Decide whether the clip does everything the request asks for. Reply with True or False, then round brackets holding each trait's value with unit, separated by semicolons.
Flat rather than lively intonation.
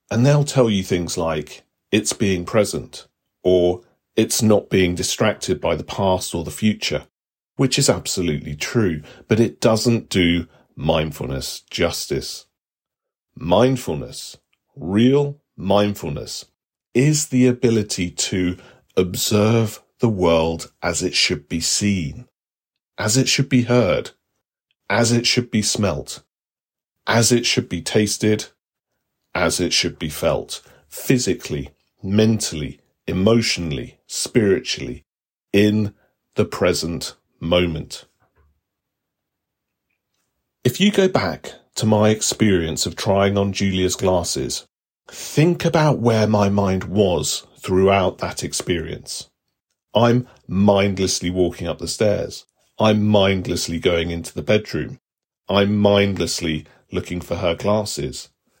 False (4.4 semitones)